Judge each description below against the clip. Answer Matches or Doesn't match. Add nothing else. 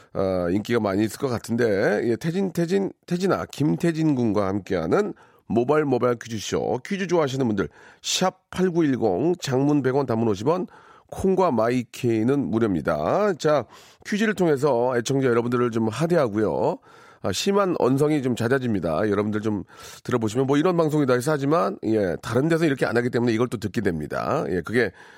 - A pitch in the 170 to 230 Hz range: Doesn't match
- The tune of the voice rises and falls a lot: Matches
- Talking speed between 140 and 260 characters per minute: Doesn't match